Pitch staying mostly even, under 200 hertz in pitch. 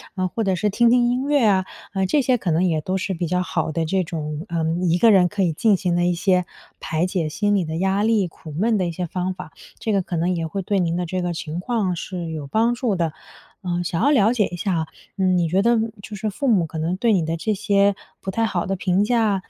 No: average, 3.5 semitones; medium, 185 Hz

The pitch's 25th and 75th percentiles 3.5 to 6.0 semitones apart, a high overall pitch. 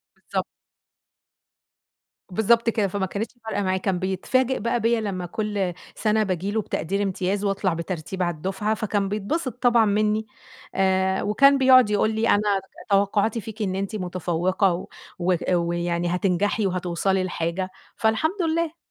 No: average, 2.9 semitones; high, 200 Hz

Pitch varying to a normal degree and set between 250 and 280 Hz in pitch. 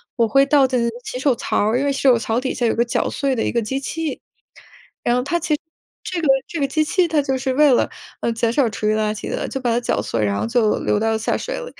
Yes: average, 3.7 semitones; very high, 255 Hz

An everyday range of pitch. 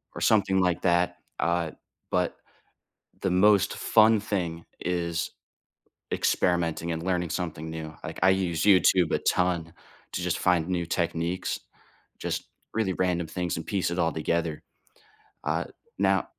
No: narrow, 1.9 semitones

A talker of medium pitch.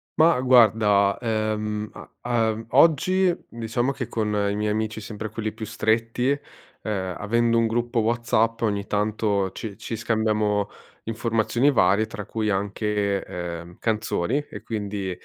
No: low, 110 Hz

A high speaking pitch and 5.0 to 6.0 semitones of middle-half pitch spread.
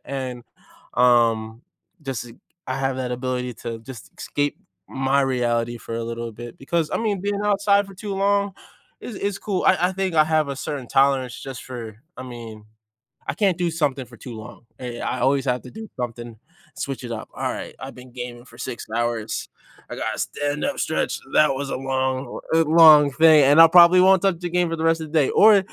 No: low, 135 Hz; average, 5.3 semitones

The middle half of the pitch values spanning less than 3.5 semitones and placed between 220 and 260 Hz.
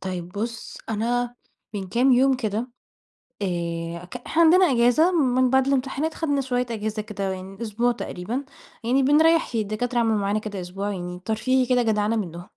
No: average, 4.4 semitones; high, 230 Hz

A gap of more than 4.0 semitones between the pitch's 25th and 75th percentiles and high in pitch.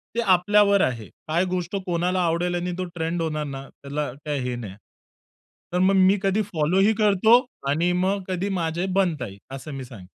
No: average, 4.4 semitones; medium, 175 Hz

